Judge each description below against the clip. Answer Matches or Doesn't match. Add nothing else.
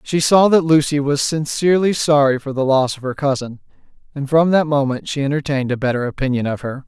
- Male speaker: Matches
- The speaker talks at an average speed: Doesn't match